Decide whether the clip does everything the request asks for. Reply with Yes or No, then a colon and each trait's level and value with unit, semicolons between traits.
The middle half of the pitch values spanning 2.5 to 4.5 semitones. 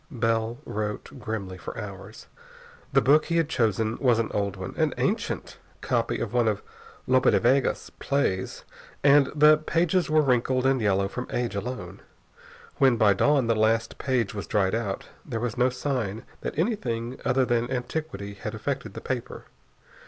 Yes: average, 3.9 semitones